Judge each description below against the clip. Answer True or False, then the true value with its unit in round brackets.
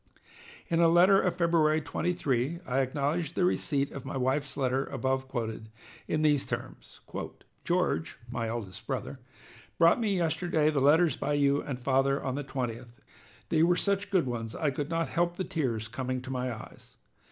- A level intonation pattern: False (4.4 semitones)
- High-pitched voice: False (140 Hz)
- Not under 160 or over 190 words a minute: True (175 wpm)